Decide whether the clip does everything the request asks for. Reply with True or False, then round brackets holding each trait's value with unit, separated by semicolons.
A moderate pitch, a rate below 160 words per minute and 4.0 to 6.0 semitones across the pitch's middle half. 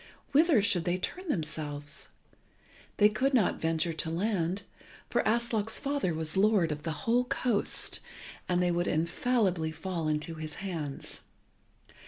True (180 Hz; 140 wpm; 5.5 semitones)